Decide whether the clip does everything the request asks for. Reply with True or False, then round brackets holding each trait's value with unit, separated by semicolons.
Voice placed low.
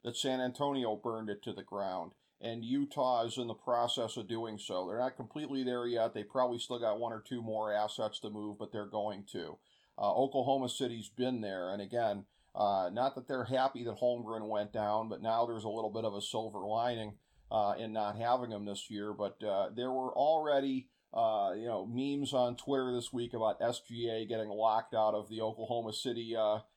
True (115 Hz)